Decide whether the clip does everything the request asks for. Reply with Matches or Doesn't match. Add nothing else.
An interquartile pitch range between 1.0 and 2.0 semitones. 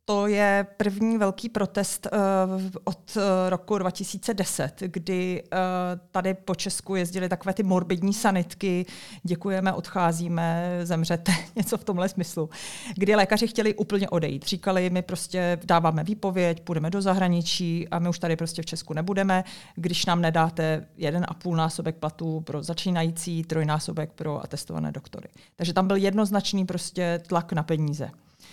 Doesn't match